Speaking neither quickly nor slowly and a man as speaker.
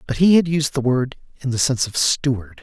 No: fast, 250 wpm; male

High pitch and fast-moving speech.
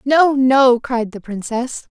No: very high, 250 Hz; average, 155 wpm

